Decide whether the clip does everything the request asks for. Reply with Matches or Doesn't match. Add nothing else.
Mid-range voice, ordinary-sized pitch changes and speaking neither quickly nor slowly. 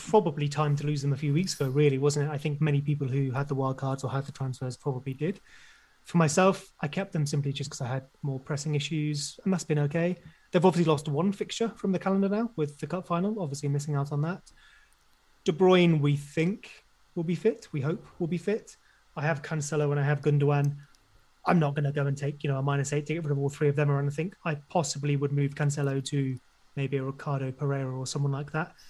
Doesn't match